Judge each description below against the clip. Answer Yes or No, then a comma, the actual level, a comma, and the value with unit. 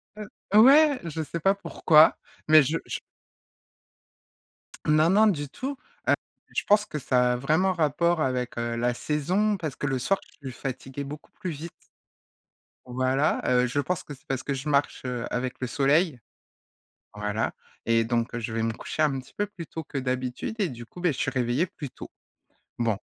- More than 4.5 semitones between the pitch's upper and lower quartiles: Yes, average, 5.1 semitones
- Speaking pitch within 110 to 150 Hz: Yes, medium, 140 Hz